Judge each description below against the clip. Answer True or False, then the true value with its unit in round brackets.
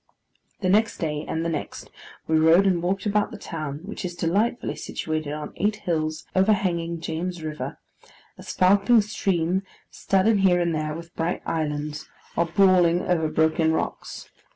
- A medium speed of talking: True (155 wpm)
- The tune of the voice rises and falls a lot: False (3.3 semitones)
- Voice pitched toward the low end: False (170 Hz)